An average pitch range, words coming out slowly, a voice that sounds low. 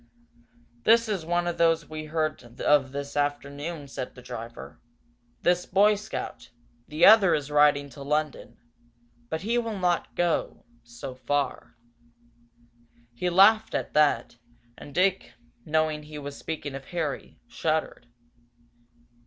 No: average, 3.6 semitones; slow, 130 wpm; medium, 155 Hz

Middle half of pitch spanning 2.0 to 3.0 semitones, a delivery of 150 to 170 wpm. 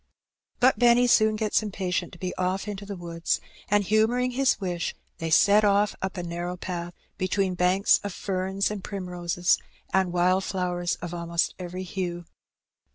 Yes: narrow, 2.6 semitones; average, 160 wpm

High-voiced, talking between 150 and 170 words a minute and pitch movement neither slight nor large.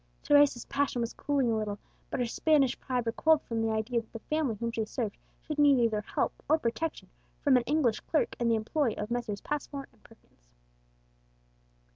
No: high, 240 Hz; average, 190 wpm; average, 4.4 semitones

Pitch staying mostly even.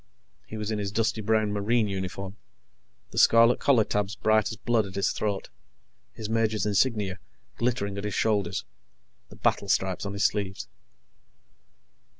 Yes: narrow, 2.0 semitones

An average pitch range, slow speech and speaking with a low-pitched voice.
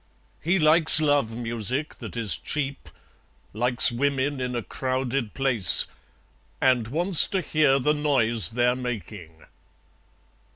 Yes: average, 3.8 semitones; slow, 120 wpm; low, 130 Hz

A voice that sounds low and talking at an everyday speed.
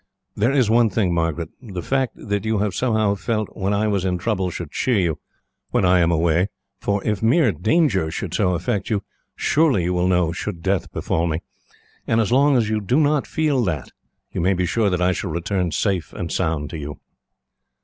No: very low, 95 Hz; fast, 210 wpm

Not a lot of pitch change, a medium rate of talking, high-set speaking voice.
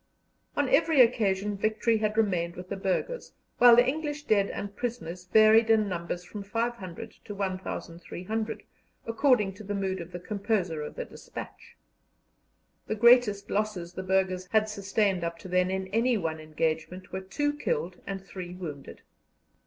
No: average, 3.7 semitones; average, 160 wpm; high, 200 Hz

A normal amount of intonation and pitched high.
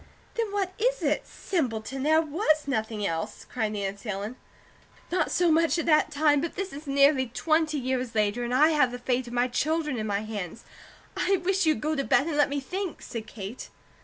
No: wide, 5.7 semitones; very high, 275 Hz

